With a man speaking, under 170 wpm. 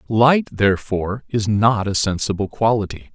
Yes: male; slow, 135 wpm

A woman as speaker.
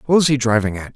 No: male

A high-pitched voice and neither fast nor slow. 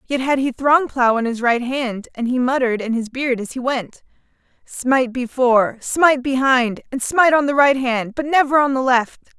No: very high, 255 Hz; fast, 210 wpm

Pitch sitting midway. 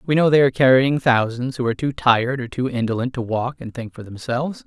No: low, 125 Hz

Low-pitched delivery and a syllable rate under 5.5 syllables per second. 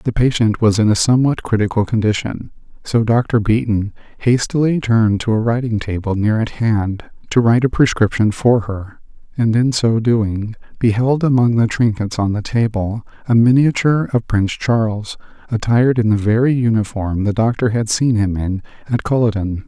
Yes: low, 115 Hz; 5.0 syllables/s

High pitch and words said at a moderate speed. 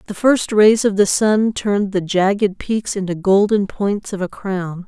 Yes: high, 200 Hz; average, 195 wpm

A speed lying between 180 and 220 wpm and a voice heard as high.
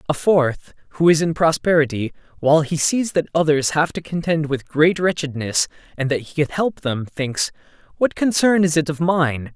No: average, 190 wpm; medium, 155 Hz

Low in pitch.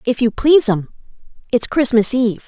No: high, 240 Hz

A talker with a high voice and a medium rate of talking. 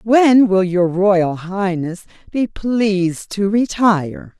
No: high, 195 Hz; slow, 125 wpm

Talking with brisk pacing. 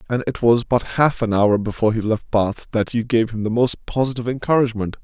Yes: fast, 225 wpm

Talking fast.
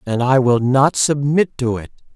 No: average, 195 wpm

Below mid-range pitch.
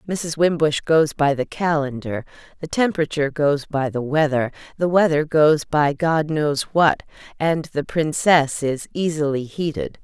No: medium, 150 Hz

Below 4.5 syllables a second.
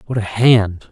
Yes: 3.9 syllables/s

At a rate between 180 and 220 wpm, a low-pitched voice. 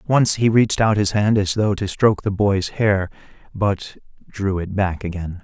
Yes: average, 200 wpm; low, 100 Hz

